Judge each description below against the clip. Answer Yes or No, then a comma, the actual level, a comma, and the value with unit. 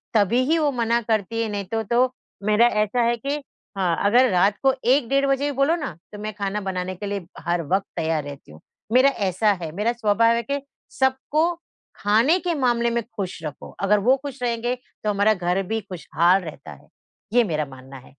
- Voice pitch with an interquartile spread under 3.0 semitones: No, average, 4.6 semitones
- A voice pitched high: Yes, high, 215 Hz